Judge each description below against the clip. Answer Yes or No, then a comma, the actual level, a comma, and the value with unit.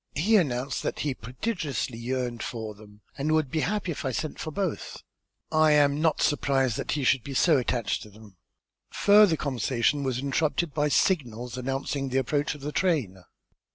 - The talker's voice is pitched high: No, medium, 140 Hz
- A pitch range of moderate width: Yes, average, 4.0 semitones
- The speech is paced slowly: No, average, 180 wpm